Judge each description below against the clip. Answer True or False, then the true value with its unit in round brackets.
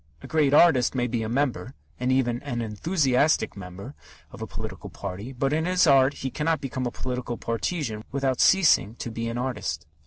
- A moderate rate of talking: True (185 wpm)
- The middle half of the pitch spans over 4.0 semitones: False (3.7 semitones)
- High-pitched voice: False (130 Hz)